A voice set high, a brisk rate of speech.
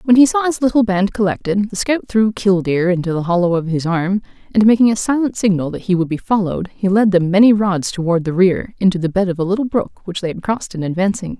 Yes: high, 195 Hz; fast, 255 wpm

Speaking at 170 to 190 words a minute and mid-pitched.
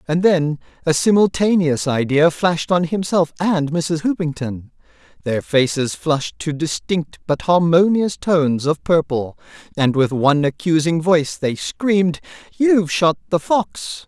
No: slow, 135 wpm; medium, 160 Hz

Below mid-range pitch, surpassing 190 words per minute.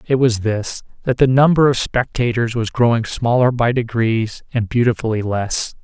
No: low, 120 Hz; average, 155 wpm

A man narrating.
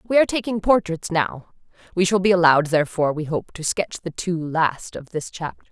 No: female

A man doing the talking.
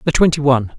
Yes: male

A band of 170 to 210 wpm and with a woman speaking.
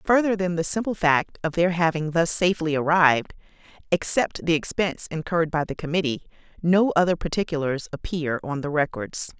No: average, 160 wpm; female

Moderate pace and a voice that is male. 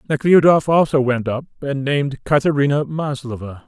No: slow, 130 wpm; male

